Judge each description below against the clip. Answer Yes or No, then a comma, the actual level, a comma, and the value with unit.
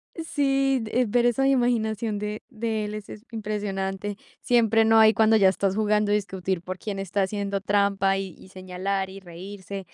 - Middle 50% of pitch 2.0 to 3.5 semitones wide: Yes, narrow, 2.5 semitones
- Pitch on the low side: No, high, 205 Hz